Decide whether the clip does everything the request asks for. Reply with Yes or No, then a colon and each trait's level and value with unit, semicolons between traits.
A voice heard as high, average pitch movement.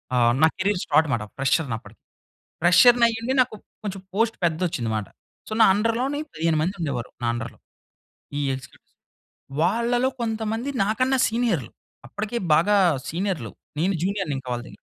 No: high, 195 Hz; wide, 7.3 semitones